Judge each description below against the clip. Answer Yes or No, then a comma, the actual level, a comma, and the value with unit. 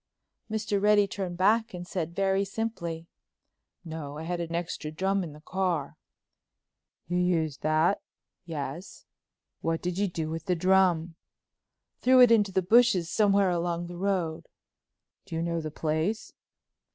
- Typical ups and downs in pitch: Yes, average, 3.2 semitones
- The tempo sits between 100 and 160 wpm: Yes, average, 150 wpm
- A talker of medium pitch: Yes, medium, 175 Hz